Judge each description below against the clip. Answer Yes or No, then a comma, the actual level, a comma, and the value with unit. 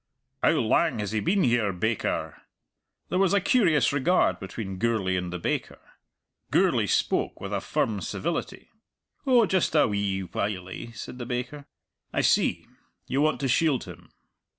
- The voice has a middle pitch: No, low, 115 Hz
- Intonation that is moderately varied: No, wide, 8.0 semitones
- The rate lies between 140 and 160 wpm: Yes, average, 155 wpm